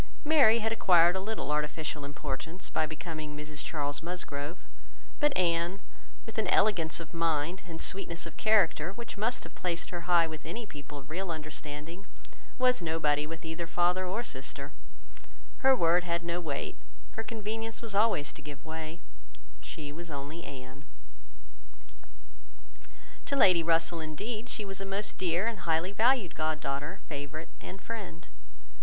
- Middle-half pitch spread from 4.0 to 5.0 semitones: Yes, average, 4.3 semitones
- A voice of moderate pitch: Yes, medium, 170 Hz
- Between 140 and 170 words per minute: Yes, average, 155 wpm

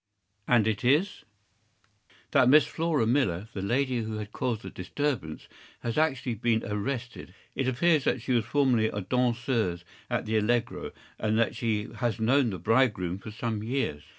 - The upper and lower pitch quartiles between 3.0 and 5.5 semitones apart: Yes, average, 3.4 semitones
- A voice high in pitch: No, low, 115 Hz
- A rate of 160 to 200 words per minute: Yes, average, 170 wpm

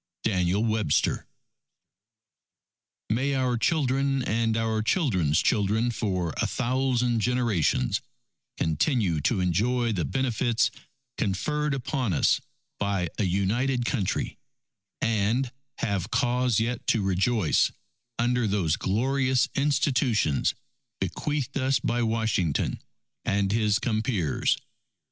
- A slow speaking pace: Yes, slow, 100 wpm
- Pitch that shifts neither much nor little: Yes, average, 4.3 semitones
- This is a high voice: No, low, 115 Hz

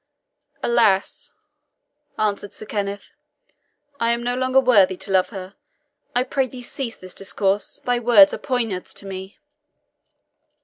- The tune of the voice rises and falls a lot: No, average, 4.0 semitones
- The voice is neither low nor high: No, high, 215 Hz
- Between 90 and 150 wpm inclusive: Yes, slow, 135 wpm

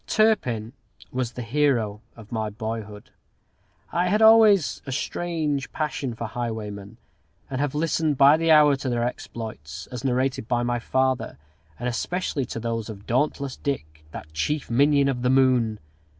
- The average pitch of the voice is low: Yes, low, 125 Hz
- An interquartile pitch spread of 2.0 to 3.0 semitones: No, average, 4.4 semitones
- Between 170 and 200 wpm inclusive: No, average, 155 wpm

